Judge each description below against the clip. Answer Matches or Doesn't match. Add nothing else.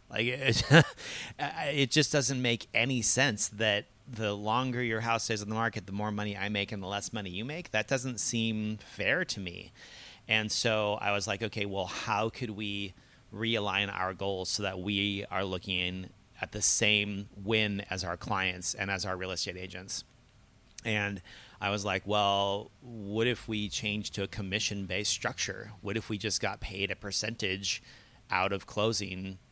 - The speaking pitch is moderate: Doesn't match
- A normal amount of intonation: Doesn't match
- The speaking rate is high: Doesn't match